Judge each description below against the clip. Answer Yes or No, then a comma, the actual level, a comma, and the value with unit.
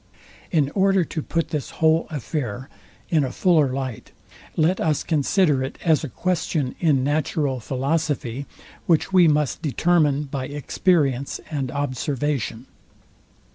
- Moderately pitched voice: Yes, medium, 150 Hz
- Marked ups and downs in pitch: No, average, 3.3 semitones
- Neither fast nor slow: No, slow, 130 wpm